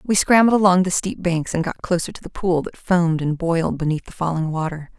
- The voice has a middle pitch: Yes, medium, 170 Hz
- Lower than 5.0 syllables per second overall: No, 5.9 syllables/s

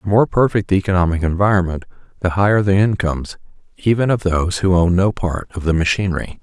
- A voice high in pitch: No, very low, 95 Hz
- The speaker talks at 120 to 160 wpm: No, average, 185 wpm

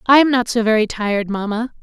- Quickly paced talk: Yes, fast, 230 wpm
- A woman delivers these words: Yes, female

